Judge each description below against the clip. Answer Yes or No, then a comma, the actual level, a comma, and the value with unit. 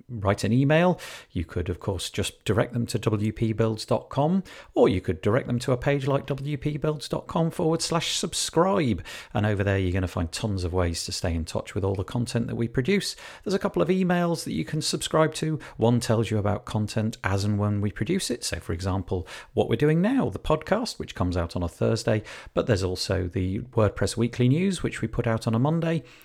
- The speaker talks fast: Yes, fast, 220 wpm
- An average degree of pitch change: No, wide, 7.0 semitones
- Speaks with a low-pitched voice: Yes, low, 115 Hz